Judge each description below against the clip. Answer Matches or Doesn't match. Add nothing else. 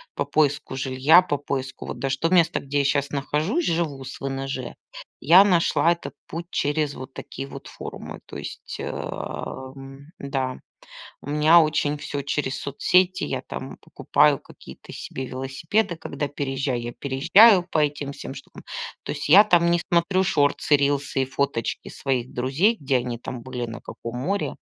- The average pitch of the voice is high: Doesn't match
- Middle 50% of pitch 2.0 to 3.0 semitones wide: Doesn't match